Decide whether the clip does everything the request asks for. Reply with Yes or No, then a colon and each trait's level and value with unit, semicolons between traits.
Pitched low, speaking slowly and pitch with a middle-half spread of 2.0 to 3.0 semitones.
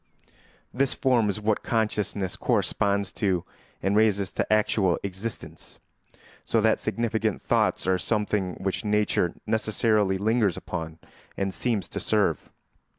Yes: low, 105 Hz; slow, 125 wpm; narrow, 2.4 semitones